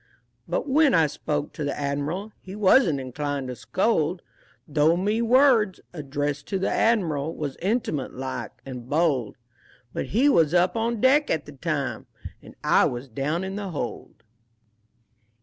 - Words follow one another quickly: No, average, 155 wpm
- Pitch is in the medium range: Yes, medium, 160 Hz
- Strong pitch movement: Yes, wide, 6.5 semitones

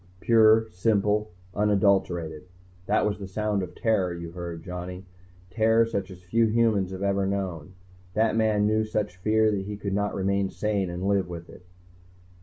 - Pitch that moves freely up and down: No, average, 2.8 semitones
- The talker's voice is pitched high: No, low, 100 Hz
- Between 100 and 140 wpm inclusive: No, average, 165 wpm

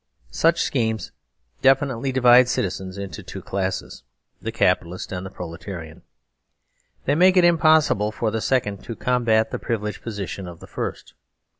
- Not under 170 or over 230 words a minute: No, average, 140 wpm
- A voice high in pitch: No, low, 110 Hz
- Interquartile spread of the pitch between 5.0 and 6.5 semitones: Yes, wide, 5.5 semitones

